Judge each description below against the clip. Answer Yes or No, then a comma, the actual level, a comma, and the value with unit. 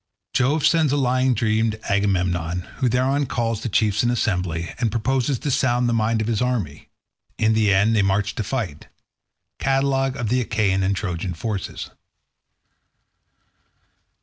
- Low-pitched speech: Yes, low, 115 Hz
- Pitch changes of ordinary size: Yes, average, 4.3 semitones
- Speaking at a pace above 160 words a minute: No, average, 150 wpm